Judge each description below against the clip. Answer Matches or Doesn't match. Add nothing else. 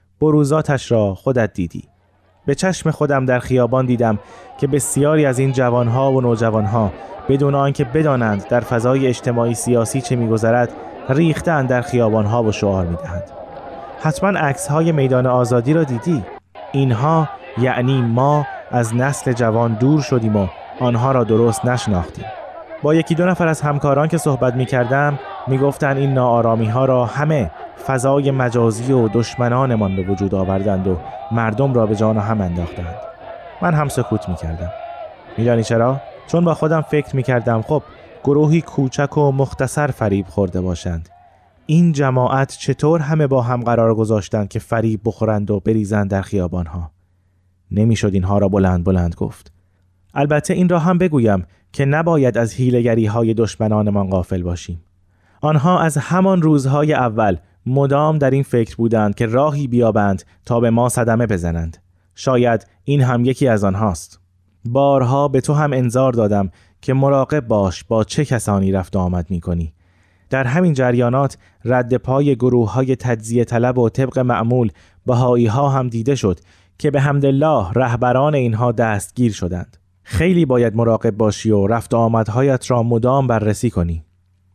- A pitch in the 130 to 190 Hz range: Doesn't match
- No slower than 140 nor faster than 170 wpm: Matches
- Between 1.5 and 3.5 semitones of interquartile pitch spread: Doesn't match